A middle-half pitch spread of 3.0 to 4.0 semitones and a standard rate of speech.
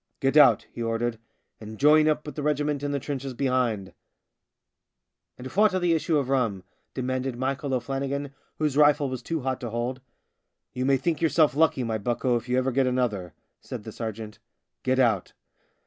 No: average, 3.3 semitones; fast, 210 wpm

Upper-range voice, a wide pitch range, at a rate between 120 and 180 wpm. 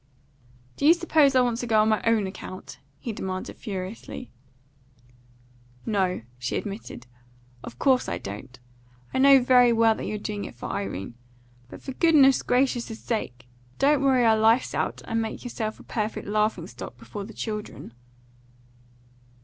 No: high, 220 Hz; average, 4.2 semitones; average, 155 wpm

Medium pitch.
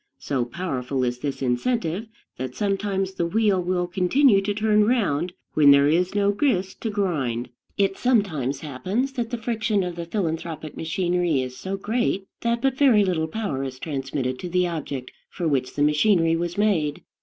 Yes: medium, 180 Hz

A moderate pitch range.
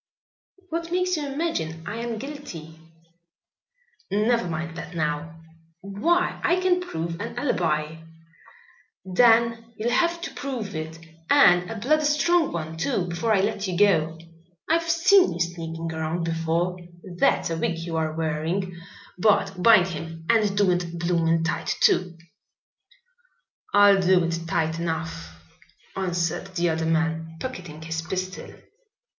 No: wide, 5.9 semitones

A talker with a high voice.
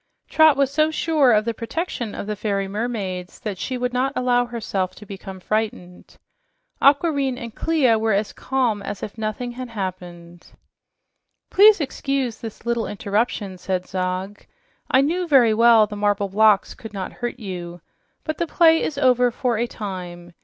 Yes: high, 225 Hz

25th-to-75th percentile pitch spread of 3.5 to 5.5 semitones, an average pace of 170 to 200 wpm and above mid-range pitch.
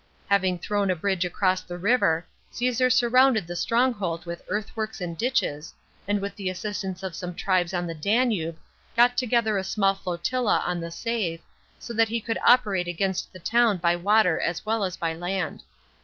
Yes: average, 4.4 semitones; average, 180 wpm; high, 195 Hz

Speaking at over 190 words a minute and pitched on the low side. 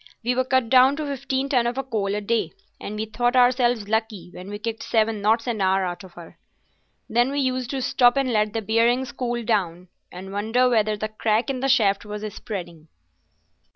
No: fast, 205 wpm; high, 225 Hz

